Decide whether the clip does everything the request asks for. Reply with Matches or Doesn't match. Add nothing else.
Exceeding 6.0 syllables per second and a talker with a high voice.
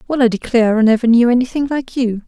Matches